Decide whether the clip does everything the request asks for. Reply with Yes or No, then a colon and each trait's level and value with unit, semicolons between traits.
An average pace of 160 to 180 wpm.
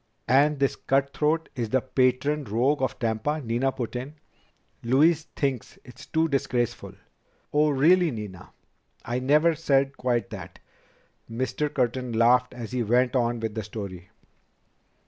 No: average, 145 wpm